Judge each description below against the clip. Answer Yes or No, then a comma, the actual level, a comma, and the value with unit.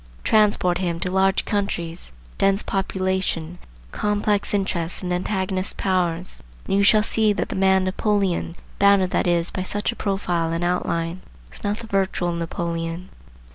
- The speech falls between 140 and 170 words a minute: Yes, average, 150 wpm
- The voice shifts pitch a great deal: No, narrow, 2.5 semitones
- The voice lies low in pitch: No, medium, 185 Hz